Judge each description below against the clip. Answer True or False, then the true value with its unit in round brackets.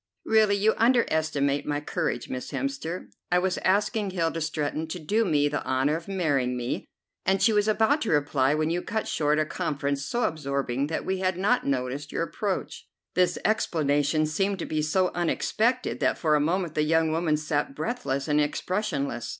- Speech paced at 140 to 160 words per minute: False (180 wpm)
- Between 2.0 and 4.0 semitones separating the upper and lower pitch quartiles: False (5.0 semitones)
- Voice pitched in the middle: True (160 Hz)